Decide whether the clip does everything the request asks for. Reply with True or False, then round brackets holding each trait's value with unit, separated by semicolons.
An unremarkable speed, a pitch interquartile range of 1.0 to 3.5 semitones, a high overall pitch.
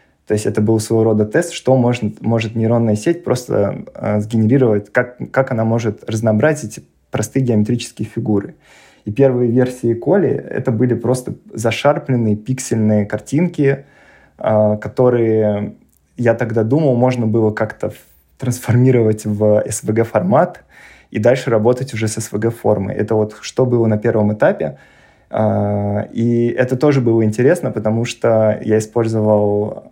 False (135 wpm; 2.7 semitones; 115 Hz)